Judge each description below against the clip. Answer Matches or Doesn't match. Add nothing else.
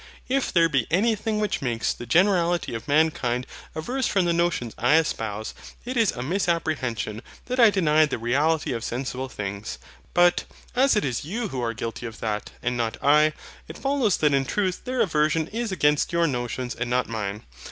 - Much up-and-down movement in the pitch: Matches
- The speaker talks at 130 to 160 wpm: Doesn't match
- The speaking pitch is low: Doesn't match